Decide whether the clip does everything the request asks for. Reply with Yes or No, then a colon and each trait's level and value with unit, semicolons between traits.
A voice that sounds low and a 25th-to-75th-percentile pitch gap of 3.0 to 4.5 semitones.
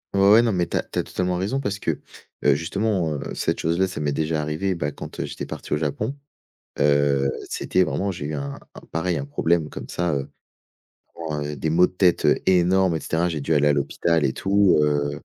Yes: very low, 80 Hz; average, 4.0 semitones